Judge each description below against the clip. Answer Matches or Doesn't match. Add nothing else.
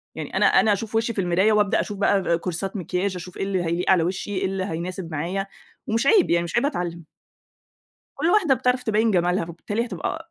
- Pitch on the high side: Matches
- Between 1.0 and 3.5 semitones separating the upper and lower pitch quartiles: Doesn't match